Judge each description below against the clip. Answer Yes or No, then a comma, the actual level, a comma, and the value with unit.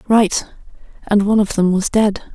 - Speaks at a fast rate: No, average, 180 wpm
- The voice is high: Yes, high, 205 Hz